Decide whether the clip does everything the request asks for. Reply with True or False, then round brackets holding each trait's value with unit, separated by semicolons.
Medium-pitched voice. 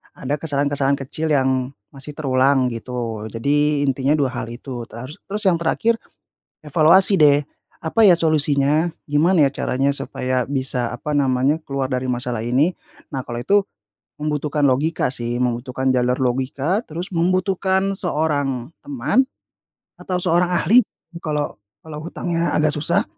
True (145 Hz)